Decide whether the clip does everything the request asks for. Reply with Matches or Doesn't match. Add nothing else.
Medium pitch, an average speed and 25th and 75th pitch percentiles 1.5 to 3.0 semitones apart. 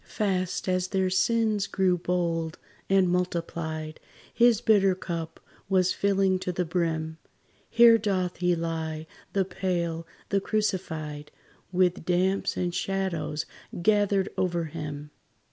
Doesn't match